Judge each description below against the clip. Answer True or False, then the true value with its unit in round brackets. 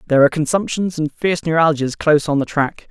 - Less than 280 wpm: True (205 wpm)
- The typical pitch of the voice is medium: True (155 Hz)